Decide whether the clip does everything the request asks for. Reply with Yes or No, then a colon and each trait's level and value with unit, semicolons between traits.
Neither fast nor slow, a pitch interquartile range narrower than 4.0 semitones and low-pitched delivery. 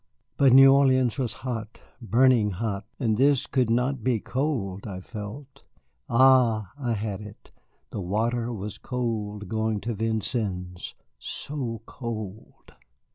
No: slow, 130 wpm; average, 3.5 semitones; low, 115 Hz